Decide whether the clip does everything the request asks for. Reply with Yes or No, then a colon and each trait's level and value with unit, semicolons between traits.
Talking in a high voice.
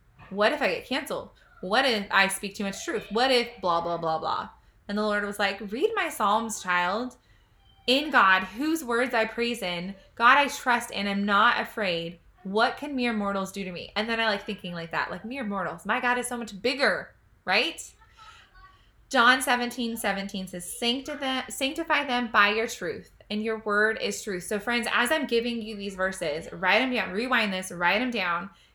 Yes: high, 220 Hz